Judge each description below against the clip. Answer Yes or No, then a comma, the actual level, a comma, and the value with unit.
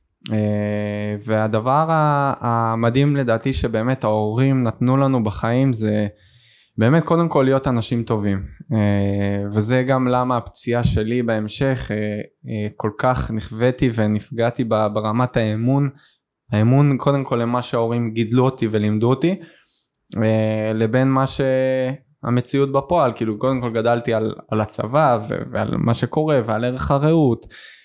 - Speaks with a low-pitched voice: Yes, low, 120 Hz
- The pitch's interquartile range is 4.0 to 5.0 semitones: No, average, 3.4 semitones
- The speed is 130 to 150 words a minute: No, average, 110 wpm